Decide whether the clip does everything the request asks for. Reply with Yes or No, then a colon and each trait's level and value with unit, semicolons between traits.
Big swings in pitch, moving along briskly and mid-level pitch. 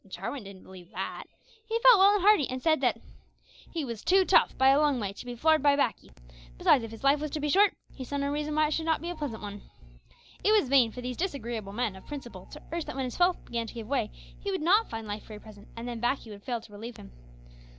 No: wide, 5.8 semitones; fast, 265 wpm; very high, 265 Hz